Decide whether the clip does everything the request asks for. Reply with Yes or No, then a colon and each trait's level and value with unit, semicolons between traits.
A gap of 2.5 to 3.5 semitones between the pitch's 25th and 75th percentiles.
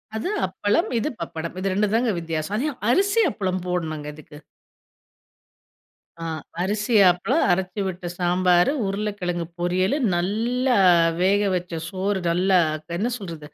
Yes: average, 3.1 semitones